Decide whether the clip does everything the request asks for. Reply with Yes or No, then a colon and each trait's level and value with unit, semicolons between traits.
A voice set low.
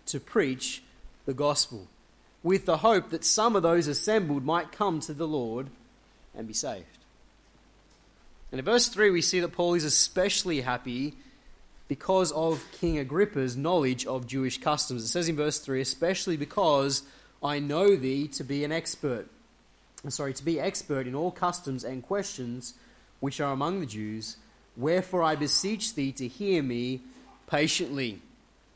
No: medium, 150 Hz